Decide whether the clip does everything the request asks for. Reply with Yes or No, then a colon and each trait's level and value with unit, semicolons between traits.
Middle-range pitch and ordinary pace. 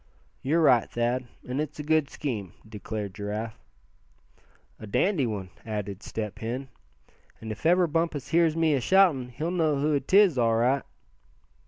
No: low, 130 Hz; average, 150 wpm